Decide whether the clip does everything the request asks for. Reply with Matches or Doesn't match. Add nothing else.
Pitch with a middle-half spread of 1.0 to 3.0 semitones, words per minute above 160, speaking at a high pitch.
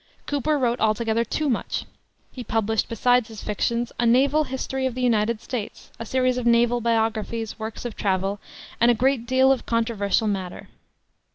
Matches